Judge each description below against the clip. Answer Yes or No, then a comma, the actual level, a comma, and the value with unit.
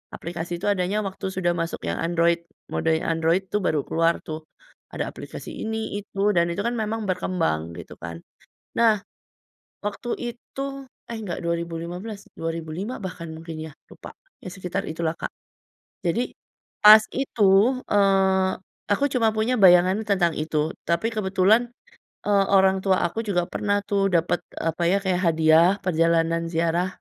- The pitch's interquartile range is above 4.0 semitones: No, average, 3.4 semitones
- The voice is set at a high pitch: No, medium, 180 Hz